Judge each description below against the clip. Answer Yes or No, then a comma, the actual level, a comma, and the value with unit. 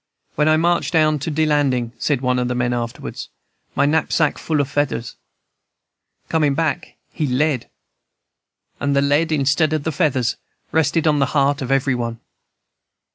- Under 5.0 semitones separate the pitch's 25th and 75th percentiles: Yes, average, 3.3 semitones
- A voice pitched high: No, medium, 145 Hz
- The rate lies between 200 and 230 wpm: No, average, 165 wpm